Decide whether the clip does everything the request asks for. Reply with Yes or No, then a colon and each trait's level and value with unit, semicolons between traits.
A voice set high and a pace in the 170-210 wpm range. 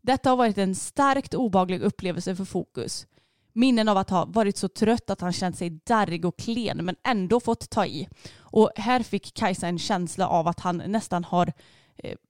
Yes: high, 195 Hz; fast, 195 wpm